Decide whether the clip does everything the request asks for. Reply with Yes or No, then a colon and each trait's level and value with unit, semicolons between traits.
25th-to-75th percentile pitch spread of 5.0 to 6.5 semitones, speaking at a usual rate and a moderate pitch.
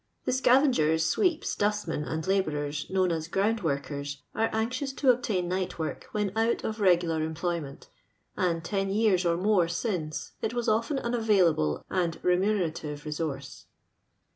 Yes: wide, 5.5 semitones; average, 155 wpm; medium, 180 Hz